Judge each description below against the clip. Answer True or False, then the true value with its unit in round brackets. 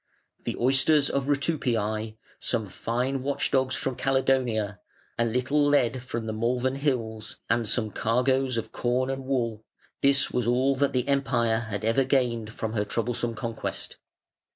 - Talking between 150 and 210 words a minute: True (155 wpm)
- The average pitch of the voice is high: False (125 Hz)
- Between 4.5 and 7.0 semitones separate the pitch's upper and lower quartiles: False (2.9 semitones)